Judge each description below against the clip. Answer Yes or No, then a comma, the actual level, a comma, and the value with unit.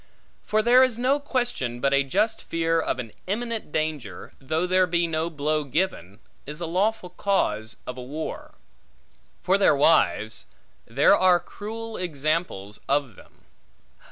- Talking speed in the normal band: Yes, average, 150 wpm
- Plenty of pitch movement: Yes, wide, 6.5 semitones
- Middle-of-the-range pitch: Yes, medium, 165 Hz